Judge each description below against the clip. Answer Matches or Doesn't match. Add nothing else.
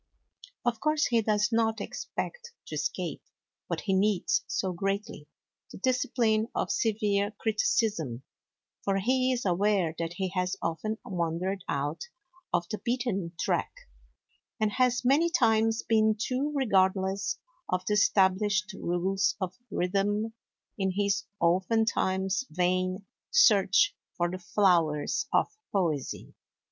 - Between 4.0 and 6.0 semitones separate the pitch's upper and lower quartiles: Doesn't match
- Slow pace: Matches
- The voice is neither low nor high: Doesn't match